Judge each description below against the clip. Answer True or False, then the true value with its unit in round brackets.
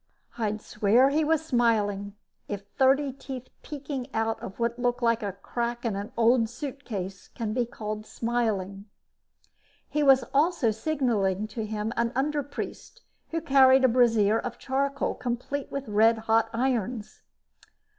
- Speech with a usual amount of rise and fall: True (3.7 semitones)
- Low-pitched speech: False (235 Hz)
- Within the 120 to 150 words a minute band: True (145 wpm)